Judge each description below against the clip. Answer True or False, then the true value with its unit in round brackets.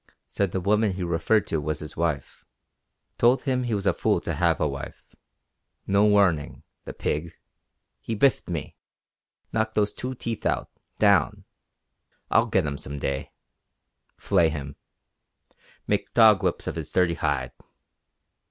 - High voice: False (85 Hz)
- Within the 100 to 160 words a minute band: True (150 wpm)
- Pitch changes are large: True (5.7 semitones)